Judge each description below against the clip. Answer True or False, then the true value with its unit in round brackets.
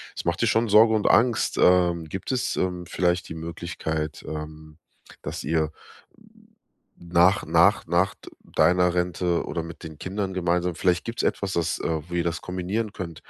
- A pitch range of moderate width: False (2.3 semitones)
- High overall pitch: False (90 Hz)